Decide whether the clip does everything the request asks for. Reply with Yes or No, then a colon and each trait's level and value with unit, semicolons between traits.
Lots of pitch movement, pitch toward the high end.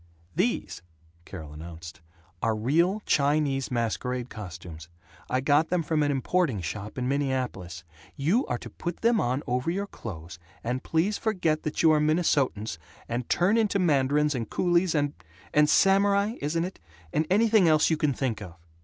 No: wide, 6.8 semitones; medium, 145 Hz